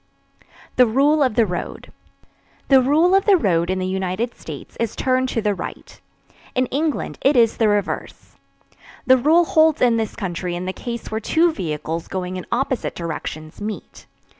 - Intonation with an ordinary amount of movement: No, wide, 6.4 semitones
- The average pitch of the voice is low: No, high, 230 Hz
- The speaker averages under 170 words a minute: No, average, 175 wpm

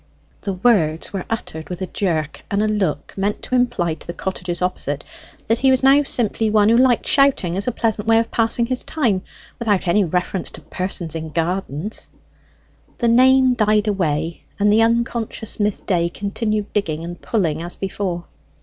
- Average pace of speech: Yes, average, 180 wpm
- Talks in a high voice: Yes, high, 205 Hz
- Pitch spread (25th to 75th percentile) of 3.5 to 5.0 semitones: Yes, average, 4.7 semitones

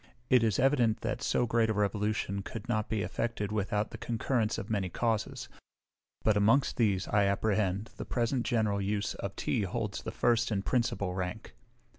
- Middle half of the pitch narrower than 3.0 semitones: Yes, narrow, 2.4 semitones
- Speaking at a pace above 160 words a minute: Yes, average, 175 wpm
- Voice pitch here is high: No, low, 110 Hz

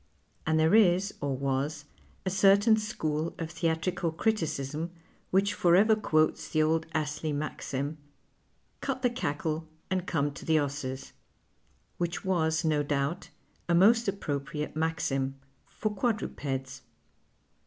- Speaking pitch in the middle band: Yes, medium, 160 Hz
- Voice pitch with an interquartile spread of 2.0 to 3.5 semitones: No, average, 4.5 semitones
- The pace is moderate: No, slow, 130 wpm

